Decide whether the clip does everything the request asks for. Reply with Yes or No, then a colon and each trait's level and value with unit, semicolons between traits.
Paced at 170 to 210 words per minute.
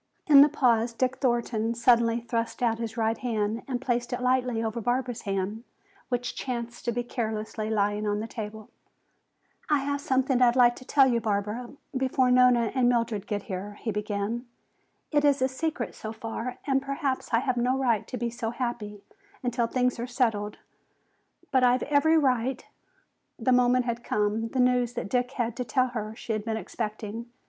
Yes: average, 185 wpm